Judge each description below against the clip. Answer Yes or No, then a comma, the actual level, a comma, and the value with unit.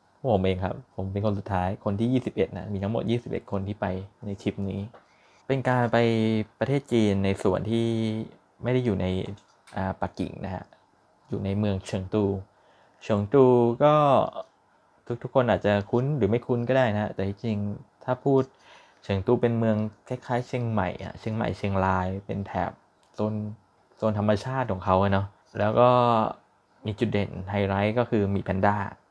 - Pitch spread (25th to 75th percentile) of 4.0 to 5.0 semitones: No, average, 3.3 semitones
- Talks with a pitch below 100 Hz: No, low, 105 Hz